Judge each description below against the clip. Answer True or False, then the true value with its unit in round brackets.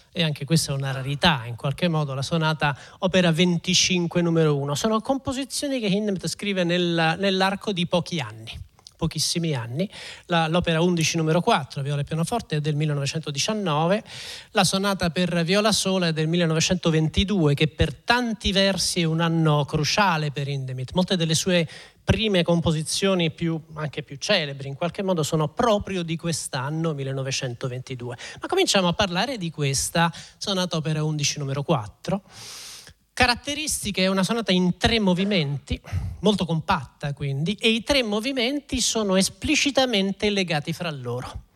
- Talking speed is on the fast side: False (150 wpm)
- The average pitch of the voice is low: False (170 Hz)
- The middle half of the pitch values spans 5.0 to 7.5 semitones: False (4.5 semitones)